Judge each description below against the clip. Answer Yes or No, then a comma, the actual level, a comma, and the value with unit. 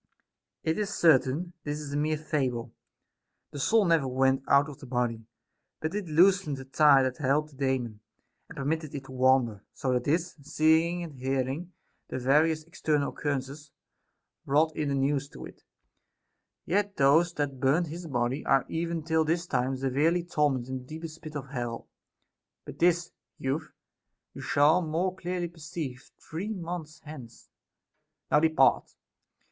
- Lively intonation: No, average, 3.6 semitones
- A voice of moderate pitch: Yes, medium, 150 Hz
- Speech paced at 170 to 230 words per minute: No, average, 160 wpm